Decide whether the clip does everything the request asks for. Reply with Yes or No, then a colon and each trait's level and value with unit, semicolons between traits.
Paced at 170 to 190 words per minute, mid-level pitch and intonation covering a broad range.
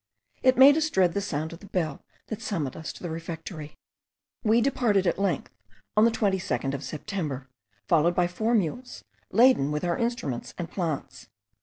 Yes: average, 175 wpm; medium, 180 Hz; wide, 5.9 semitones